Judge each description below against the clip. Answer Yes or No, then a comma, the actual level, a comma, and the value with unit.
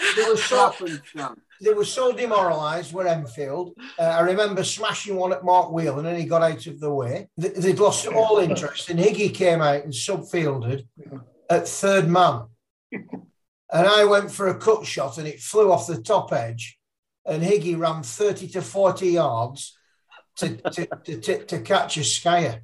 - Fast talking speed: No, average, 180 wpm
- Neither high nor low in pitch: Yes, medium, 175 Hz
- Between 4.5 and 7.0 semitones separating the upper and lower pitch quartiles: Yes, average, 4.9 semitones